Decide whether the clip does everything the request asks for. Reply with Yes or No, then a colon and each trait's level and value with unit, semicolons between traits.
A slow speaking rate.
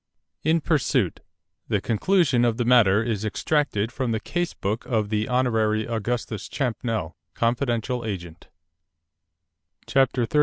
Yes: slow, 125 wpm